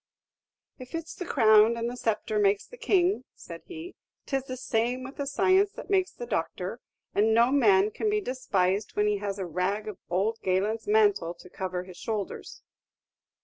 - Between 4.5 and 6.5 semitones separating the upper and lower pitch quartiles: Yes, average, 5.3 semitones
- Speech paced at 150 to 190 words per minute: Yes, average, 185 wpm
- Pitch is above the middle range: Yes, high, 220 Hz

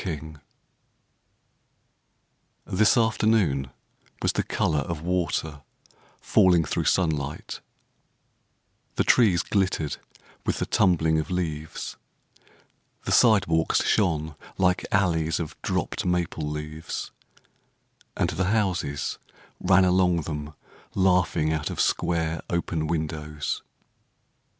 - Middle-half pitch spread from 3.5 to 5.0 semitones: No, average, 3.1 semitones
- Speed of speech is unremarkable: No, slow, 100 wpm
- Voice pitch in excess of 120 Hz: No, very low, 80 Hz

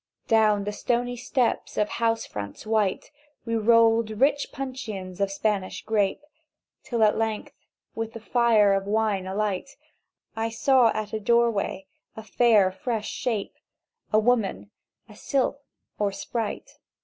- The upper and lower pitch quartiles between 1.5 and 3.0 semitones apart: Yes, narrow, 2.4 semitones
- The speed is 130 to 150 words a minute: Yes, average, 145 wpm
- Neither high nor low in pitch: No, high, 220 Hz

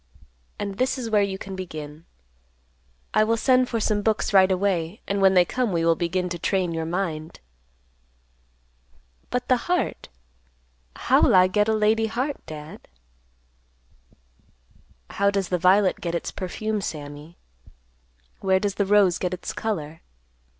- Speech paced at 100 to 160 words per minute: Yes, average, 150 wpm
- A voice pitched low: No, high, 190 Hz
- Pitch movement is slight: No, average, 3.9 semitones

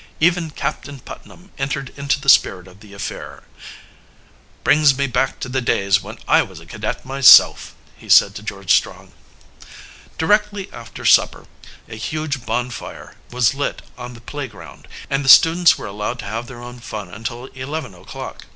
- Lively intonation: No, average, 4.3 semitones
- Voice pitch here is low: Yes, low, 125 Hz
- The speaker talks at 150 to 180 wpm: Yes, average, 165 wpm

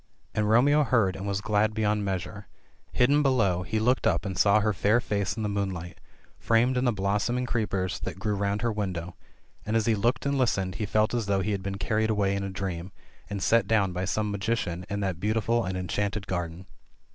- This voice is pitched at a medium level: No, low, 105 Hz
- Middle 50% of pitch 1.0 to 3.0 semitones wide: Yes, average, 2.7 semitones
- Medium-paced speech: No, fast, 215 wpm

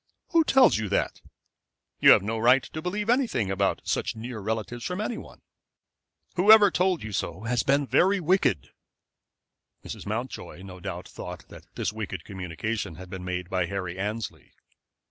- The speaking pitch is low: Yes, low, 110 Hz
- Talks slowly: No, average, 165 wpm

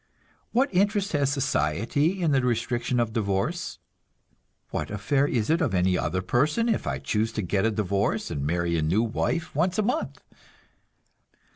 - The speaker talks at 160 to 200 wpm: Yes, average, 165 wpm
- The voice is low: Yes, low, 120 Hz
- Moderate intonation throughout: No, wide, 8.7 semitones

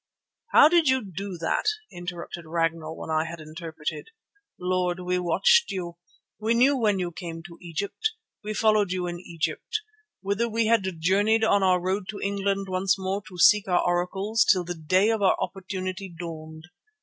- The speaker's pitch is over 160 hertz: Yes, medium, 185 Hz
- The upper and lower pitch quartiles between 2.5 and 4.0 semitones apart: Yes, average, 3.0 semitones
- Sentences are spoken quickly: No, average, 175 wpm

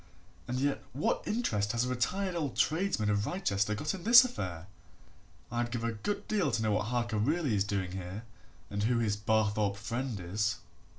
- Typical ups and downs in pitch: No, wide, 5.9 semitones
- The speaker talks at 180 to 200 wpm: Yes, average, 185 wpm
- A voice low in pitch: Yes, low, 115 Hz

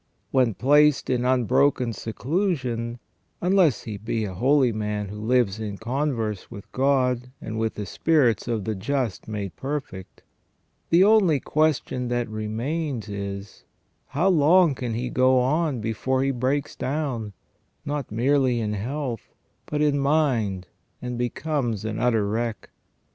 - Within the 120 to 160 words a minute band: Yes, average, 140 wpm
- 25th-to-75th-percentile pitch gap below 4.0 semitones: No, average, 4.6 semitones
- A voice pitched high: No, low, 125 Hz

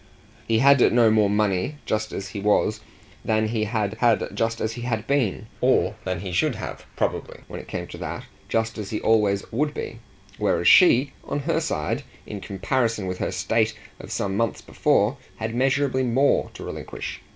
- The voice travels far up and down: No, average, 3.1 semitones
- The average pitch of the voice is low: Yes, low, 110 Hz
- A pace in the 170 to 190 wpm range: Yes, average, 185 wpm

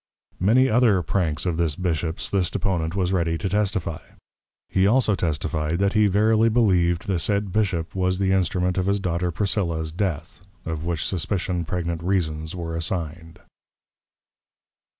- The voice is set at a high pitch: No, very low, 90 Hz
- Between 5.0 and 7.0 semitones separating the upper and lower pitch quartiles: No, average, 3.1 semitones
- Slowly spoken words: No, average, 150 wpm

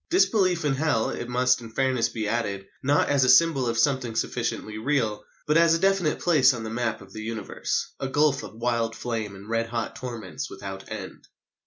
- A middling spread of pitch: Yes, average, 4.3 semitones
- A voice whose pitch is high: No, low, 120 Hz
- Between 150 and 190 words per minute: No, average, 200 wpm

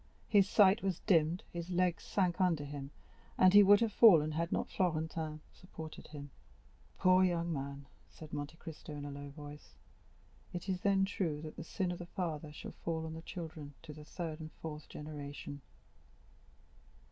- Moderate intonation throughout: Yes, average, 3.4 semitones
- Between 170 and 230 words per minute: Yes, average, 175 wpm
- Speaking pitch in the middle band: Yes, medium, 160 Hz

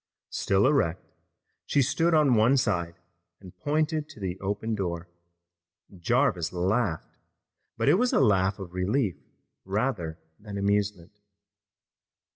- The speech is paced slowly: Yes, slow, 120 wpm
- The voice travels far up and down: Yes, wide, 6.0 semitones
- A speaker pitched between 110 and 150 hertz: No, low, 100 Hz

